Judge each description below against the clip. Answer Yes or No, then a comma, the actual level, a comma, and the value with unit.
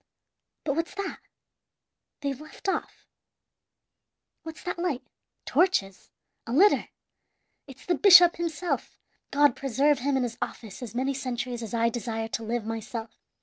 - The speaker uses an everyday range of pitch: No, wide, 5.7 semitones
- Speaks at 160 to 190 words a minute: No, average, 140 wpm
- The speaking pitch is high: Yes, very high, 265 Hz